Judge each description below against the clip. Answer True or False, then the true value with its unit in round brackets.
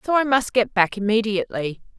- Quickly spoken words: False (180 wpm)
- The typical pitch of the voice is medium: False (220 Hz)